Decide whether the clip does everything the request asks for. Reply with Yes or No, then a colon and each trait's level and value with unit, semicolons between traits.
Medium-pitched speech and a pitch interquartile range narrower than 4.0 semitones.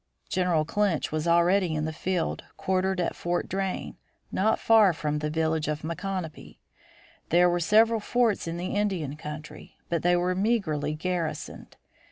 Yes: medium, 175 Hz; average, 3.4 semitones